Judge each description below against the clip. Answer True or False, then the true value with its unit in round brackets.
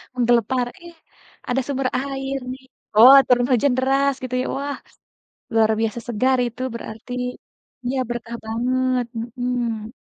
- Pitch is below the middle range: False (250 Hz)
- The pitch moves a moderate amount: False (2.0 semitones)